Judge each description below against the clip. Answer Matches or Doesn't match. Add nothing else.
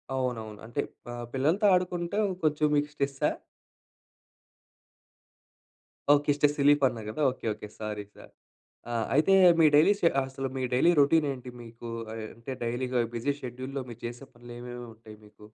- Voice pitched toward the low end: Matches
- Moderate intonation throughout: Matches